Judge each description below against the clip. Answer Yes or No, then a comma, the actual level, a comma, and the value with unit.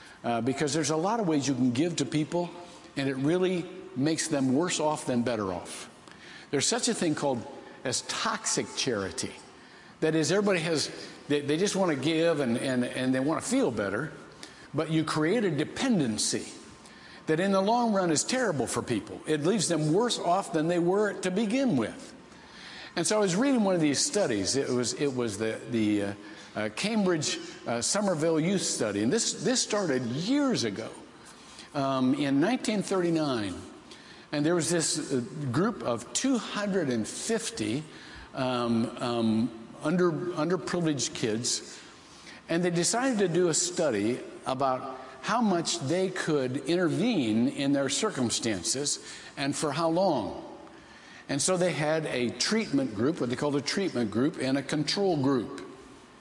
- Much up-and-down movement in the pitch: Yes, wide, 6.0 semitones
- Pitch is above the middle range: No, medium, 160 Hz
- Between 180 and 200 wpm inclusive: No, average, 165 wpm